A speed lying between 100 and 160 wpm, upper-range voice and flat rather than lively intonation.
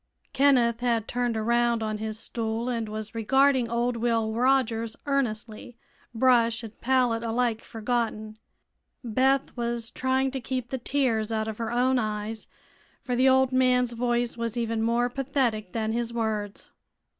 Yes: average, 150 wpm; high, 235 Hz; narrow, 2.1 semitones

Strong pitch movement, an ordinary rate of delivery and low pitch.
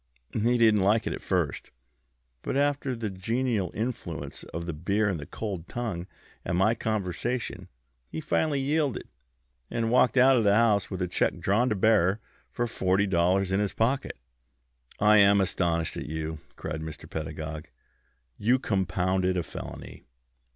No: average, 4.7 semitones; average, 160 wpm; low, 100 Hz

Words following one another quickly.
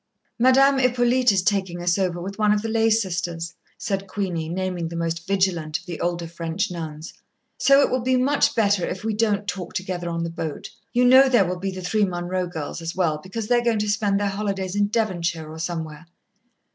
Yes: fast, 215 wpm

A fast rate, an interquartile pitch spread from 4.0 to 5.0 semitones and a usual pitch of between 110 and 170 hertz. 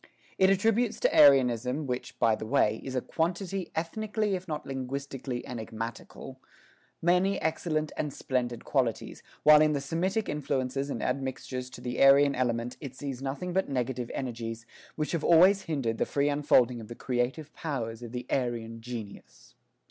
No: average, 160 wpm; average, 4.5 semitones; low, 135 Hz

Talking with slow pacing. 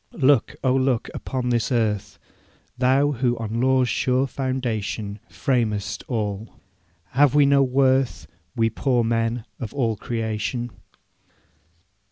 Yes: slow, 120 wpm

